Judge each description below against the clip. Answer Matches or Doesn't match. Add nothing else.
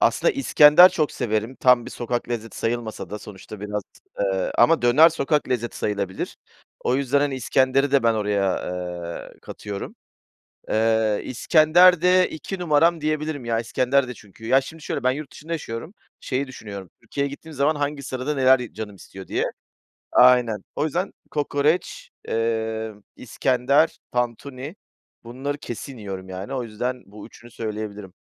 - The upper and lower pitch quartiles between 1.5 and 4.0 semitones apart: Doesn't match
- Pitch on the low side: Matches